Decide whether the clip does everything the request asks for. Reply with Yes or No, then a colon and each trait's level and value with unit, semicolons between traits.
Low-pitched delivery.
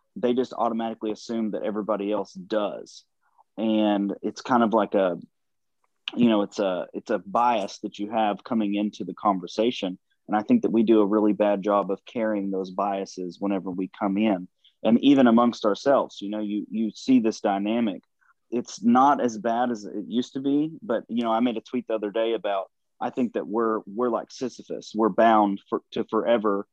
Yes: low, 110 Hz